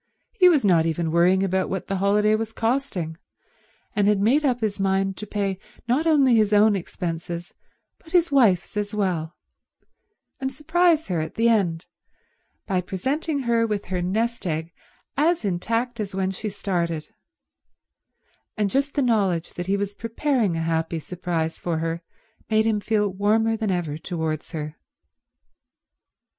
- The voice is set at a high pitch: Yes, high, 200 Hz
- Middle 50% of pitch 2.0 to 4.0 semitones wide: No, average, 4.6 semitones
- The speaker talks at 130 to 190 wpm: Yes, average, 155 wpm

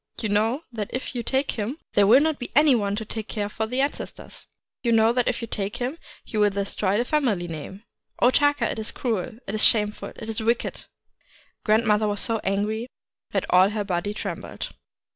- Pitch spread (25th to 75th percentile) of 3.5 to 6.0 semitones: No, average, 3.1 semitones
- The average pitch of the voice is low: No, high, 220 Hz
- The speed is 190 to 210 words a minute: Yes, fast, 205 wpm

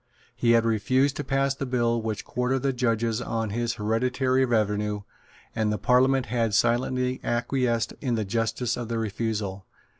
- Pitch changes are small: Yes, narrow, 2.3 semitones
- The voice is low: Yes, low, 115 Hz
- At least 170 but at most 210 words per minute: No, average, 160 wpm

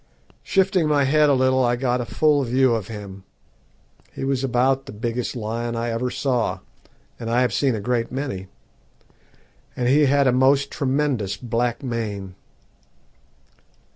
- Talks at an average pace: Yes, average, 155 wpm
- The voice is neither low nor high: No, low, 125 Hz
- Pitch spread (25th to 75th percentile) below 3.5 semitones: Yes, average, 2.8 semitones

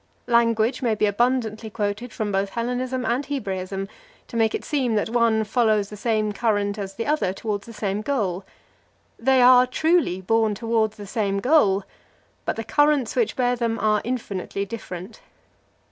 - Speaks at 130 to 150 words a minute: No, average, 165 wpm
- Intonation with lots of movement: No, average, 3.3 semitones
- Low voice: No, high, 225 Hz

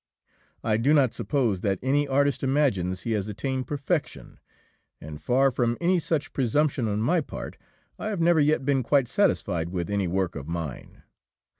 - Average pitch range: No, wide, 6.7 semitones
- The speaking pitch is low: Yes, low, 130 Hz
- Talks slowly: No, average, 170 wpm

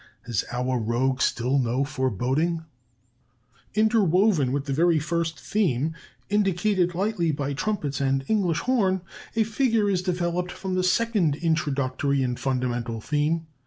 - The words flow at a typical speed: No, slow, 130 wpm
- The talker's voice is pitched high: No, medium, 160 Hz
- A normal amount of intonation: No, wide, 5.9 semitones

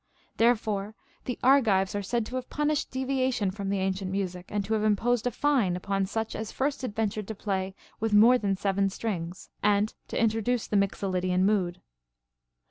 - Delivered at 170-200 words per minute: Yes, average, 175 wpm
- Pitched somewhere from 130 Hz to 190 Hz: No, high, 210 Hz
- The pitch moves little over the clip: No, average, 3.4 semitones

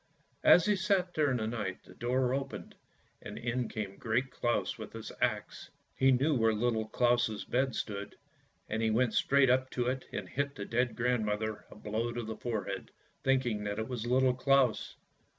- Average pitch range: Yes, average, 3.1 semitones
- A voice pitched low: Yes, low, 120 Hz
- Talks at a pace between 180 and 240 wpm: Yes, average, 190 wpm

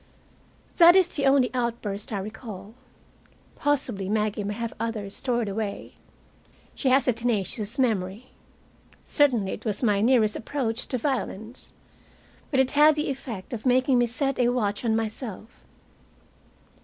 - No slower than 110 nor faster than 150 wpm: Yes, average, 145 wpm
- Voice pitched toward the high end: Yes, high, 235 Hz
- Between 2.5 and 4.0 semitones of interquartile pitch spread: Yes, average, 3.7 semitones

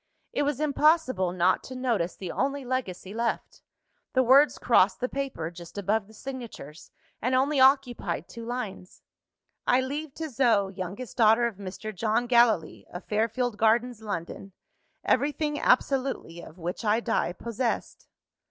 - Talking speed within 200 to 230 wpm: No, average, 145 wpm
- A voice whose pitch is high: Yes, high, 235 Hz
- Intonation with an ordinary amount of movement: Yes, average, 5.0 semitones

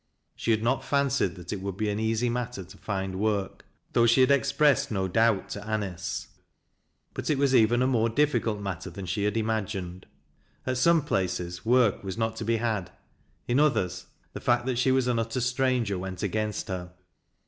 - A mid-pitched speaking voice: No, low, 110 Hz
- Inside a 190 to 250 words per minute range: Yes, average, 195 wpm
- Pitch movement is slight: No, average, 4.3 semitones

